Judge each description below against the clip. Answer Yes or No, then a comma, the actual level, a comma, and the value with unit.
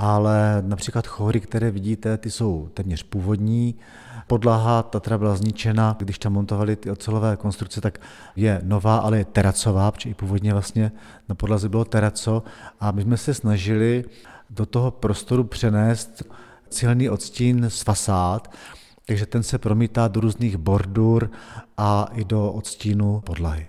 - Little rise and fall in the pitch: Yes, narrow, 1.8 semitones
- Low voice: Yes, low, 110 Hz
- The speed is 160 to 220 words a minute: No, average, 145 wpm